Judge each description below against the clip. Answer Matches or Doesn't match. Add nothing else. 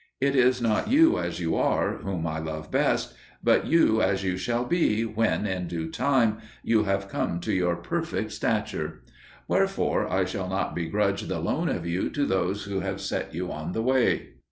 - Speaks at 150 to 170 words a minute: Doesn't match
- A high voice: Doesn't match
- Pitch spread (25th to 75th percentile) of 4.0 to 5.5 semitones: Matches